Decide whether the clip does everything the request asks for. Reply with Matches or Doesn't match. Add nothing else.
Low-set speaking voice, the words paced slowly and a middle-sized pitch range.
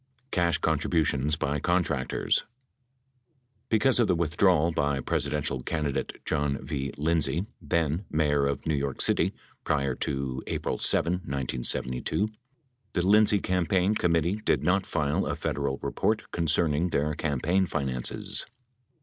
Matches